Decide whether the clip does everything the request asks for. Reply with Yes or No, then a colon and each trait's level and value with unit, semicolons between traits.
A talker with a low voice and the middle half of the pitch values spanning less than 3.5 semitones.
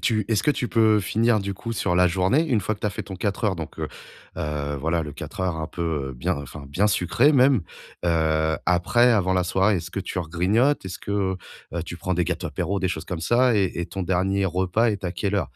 No: very low, 95 Hz; average, 3.8 semitones